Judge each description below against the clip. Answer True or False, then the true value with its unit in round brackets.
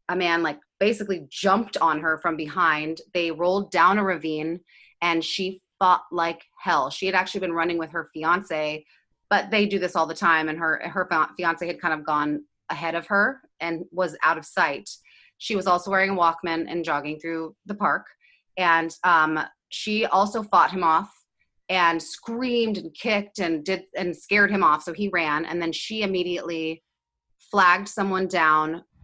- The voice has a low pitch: False (175 Hz)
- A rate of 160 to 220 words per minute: True (180 wpm)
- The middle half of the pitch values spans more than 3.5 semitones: False (3.0 semitones)